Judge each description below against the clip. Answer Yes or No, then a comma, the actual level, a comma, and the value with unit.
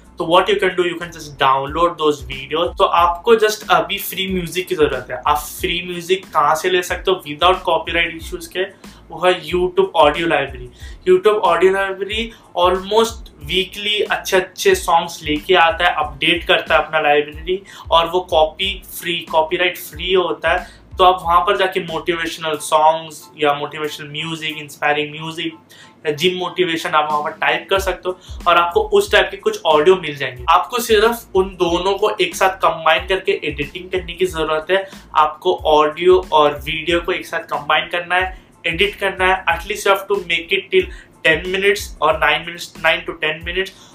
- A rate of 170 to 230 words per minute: Yes, average, 185 wpm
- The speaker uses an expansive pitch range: No, average, 3.3 semitones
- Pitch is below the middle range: No, medium, 175 Hz